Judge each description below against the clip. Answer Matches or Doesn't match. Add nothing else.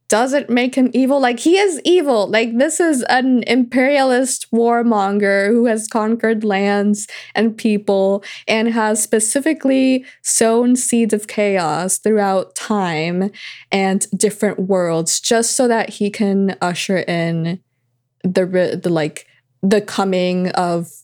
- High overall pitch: Matches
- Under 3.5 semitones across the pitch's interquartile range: Doesn't match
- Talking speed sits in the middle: Doesn't match